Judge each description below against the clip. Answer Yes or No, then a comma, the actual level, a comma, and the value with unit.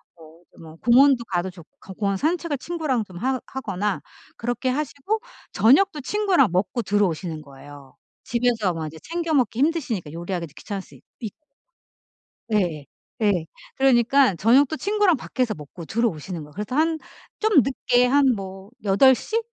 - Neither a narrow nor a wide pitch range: No, wide, 7.3 semitones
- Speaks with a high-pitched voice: Yes, high, 230 Hz